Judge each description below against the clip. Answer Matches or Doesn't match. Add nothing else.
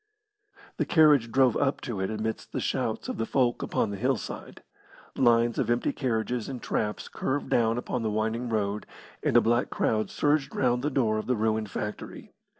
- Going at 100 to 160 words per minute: Doesn't match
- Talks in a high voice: Doesn't match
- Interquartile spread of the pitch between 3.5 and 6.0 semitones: Doesn't match